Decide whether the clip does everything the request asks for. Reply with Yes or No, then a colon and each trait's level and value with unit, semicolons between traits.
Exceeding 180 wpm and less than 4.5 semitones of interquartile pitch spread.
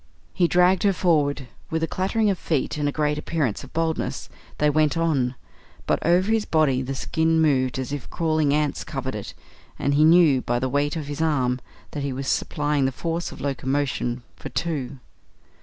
Yes: average, 190 wpm; average, 3.3 semitones